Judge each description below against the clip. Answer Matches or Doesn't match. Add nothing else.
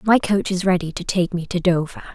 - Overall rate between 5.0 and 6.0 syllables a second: Matches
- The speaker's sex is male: Doesn't match